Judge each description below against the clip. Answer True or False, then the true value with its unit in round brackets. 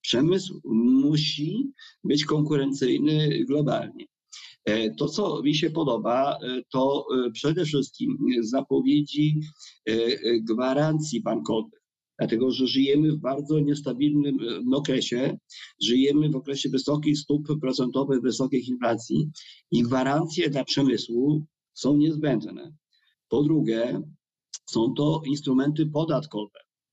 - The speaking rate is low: True (95 wpm)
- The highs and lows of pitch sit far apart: False (2.7 semitones)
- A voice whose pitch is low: False (145 Hz)